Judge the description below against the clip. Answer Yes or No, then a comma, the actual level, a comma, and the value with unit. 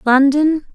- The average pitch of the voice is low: No, very high, 285 Hz